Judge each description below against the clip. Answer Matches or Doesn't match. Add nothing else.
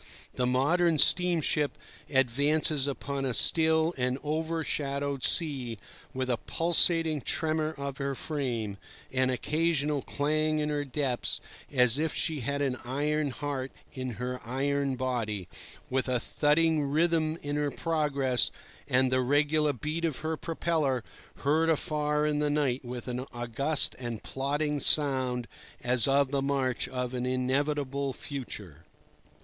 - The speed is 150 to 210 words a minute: Doesn't match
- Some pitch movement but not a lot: Matches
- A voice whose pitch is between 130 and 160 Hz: Matches